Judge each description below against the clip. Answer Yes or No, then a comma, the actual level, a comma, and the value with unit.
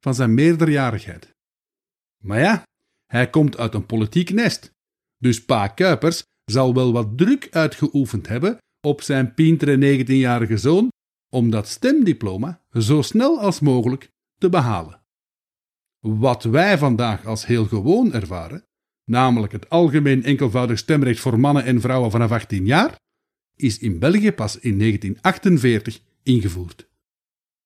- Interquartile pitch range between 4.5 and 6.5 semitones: Yes, wide, 5.6 semitones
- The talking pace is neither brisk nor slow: No, slow, 130 wpm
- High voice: No, low, 130 Hz